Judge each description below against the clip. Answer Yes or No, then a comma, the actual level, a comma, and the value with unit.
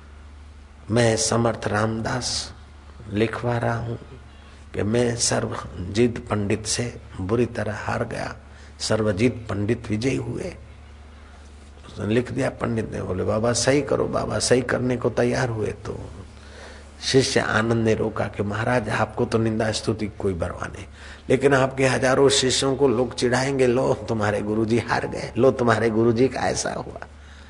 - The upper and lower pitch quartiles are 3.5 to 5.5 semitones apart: Yes, average, 4.8 semitones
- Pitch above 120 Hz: No, low, 110 Hz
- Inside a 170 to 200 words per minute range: No, average, 145 wpm